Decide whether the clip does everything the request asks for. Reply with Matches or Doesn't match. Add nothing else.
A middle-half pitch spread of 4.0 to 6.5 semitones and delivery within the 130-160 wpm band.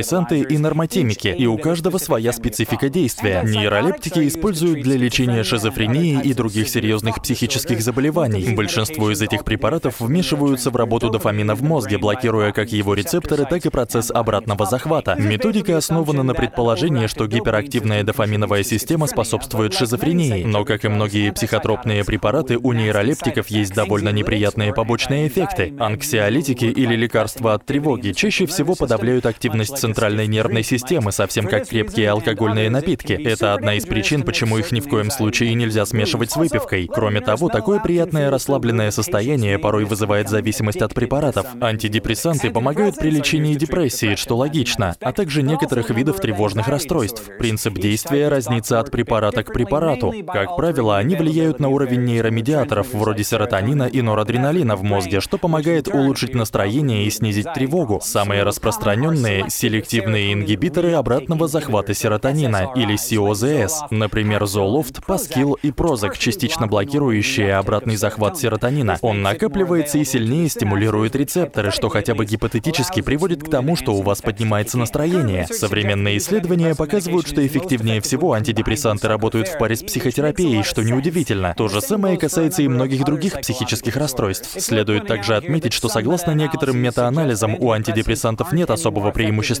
Matches